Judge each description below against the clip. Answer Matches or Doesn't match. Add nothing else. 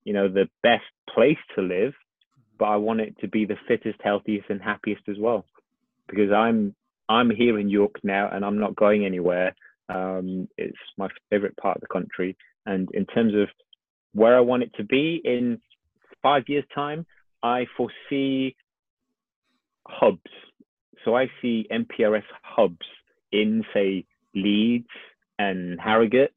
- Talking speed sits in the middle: Matches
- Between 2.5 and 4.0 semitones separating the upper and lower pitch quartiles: Matches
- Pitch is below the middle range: Matches